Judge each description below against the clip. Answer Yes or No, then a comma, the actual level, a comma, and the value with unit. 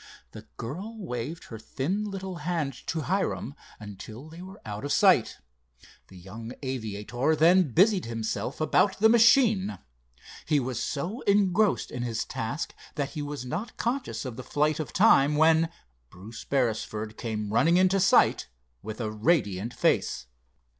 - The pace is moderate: Yes, average, 150 wpm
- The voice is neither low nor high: Yes, medium, 145 Hz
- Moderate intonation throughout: No, wide, 8.3 semitones